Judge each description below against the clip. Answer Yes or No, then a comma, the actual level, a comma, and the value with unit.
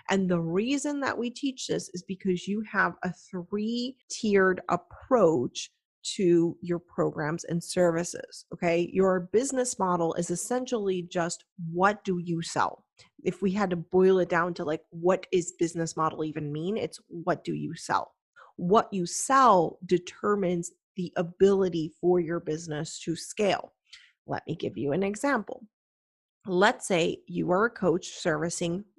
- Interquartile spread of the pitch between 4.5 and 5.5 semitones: No, average, 3.2 semitones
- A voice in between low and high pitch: Yes, medium, 180 Hz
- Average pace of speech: Yes, average, 155 wpm